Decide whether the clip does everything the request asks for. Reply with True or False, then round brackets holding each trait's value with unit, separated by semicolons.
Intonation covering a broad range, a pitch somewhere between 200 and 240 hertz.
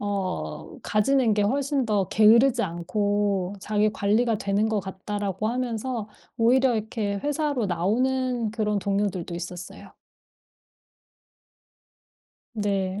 False (3.3 semitones; 210 Hz)